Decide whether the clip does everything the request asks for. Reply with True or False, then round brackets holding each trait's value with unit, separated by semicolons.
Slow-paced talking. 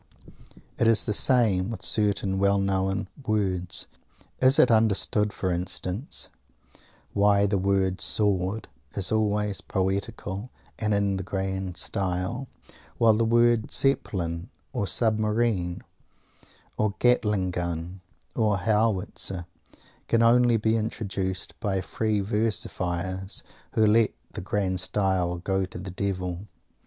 True (120 wpm)